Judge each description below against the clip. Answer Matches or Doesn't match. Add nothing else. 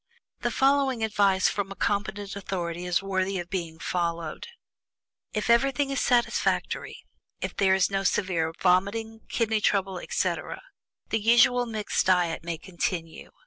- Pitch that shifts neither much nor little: Matches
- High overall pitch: Matches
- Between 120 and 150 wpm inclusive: Matches